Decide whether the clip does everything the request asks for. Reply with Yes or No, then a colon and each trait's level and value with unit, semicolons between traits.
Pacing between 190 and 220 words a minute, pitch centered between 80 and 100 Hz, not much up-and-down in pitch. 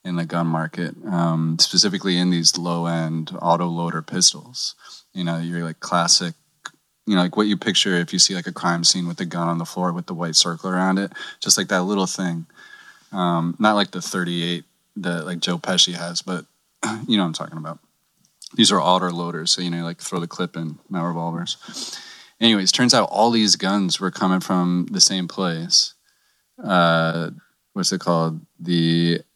Yes: average, 195 wpm; very low, 85 Hz; narrow, 1.5 semitones